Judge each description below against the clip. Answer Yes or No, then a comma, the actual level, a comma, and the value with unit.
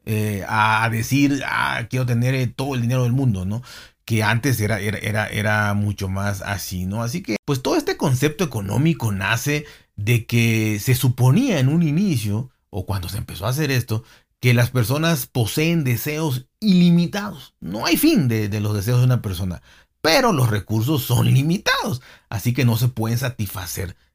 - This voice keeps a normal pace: Yes, average, 175 wpm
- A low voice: Yes, low, 120 Hz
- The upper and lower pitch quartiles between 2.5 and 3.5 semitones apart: No, average, 4.4 semitones